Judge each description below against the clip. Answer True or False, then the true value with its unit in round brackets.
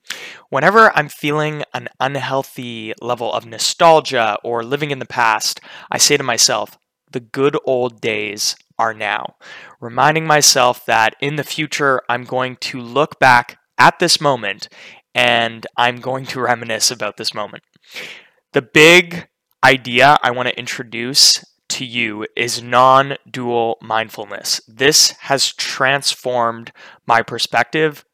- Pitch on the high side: False (125 Hz)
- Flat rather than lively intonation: False (3.2 semitones)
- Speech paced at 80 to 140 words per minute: True (135 wpm)